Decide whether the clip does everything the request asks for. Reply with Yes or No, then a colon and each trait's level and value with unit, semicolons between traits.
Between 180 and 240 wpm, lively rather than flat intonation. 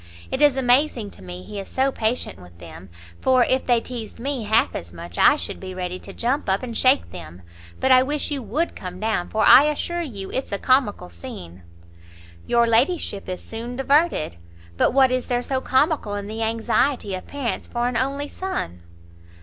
Yes: average, 200 wpm; wide, 5.7 semitones